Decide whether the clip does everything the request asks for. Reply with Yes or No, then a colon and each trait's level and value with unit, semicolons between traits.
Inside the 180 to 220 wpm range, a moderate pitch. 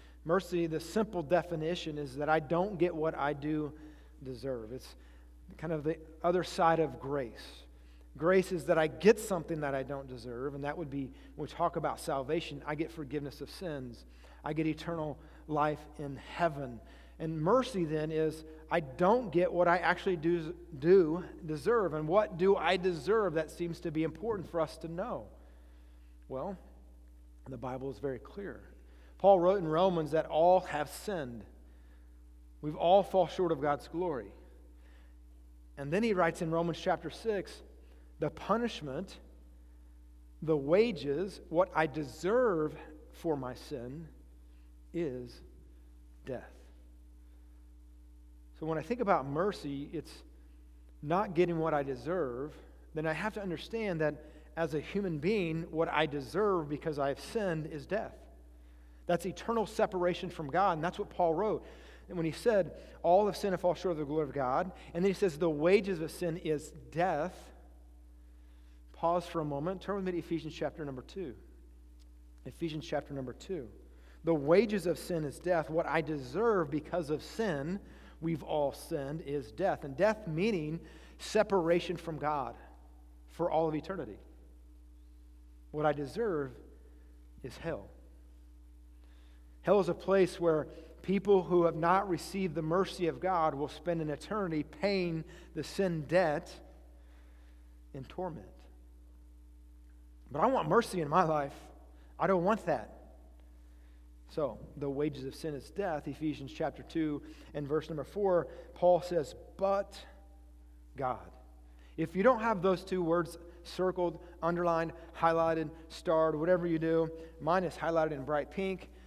No: average, 155 wpm; medium, 155 Hz